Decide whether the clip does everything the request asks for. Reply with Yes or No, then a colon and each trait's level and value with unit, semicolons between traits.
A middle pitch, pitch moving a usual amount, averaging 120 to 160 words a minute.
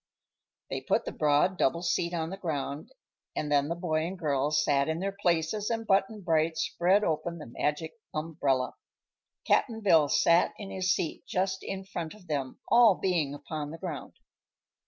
No: medium, 165 Hz; average, 4.0 semitones; average, 175 wpm